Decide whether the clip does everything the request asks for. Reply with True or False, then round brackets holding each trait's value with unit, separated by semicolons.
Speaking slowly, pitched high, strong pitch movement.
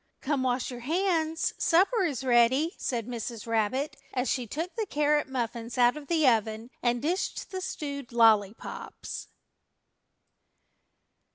False (130 wpm; 260 Hz; 5.0 semitones)